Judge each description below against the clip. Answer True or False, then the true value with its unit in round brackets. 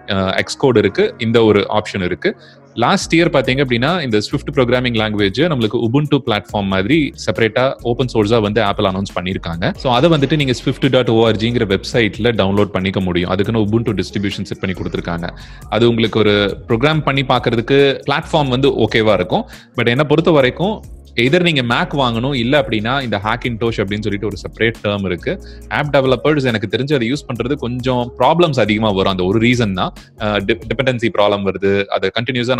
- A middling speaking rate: False (145 wpm)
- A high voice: False (115 Hz)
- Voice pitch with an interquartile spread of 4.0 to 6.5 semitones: True (4.3 semitones)